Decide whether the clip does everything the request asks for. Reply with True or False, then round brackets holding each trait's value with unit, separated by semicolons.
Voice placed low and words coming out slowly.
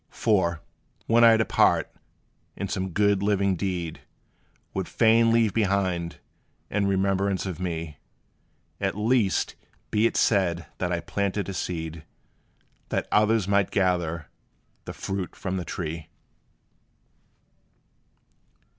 True (95 Hz; 115 wpm)